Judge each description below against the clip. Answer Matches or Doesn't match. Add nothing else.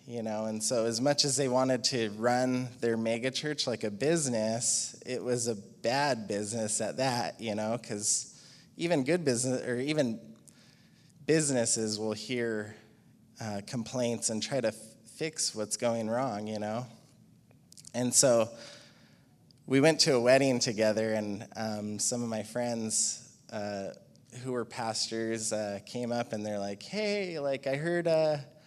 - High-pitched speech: Doesn't match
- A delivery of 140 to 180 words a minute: Matches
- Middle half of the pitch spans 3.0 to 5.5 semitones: Matches